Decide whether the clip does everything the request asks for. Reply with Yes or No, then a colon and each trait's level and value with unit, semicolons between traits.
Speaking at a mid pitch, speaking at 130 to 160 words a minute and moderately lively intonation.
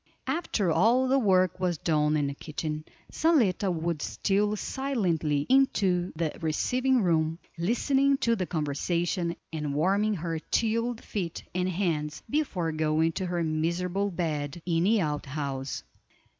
Yes: medium, 175 Hz; average, 140 wpm; average, 5.0 semitones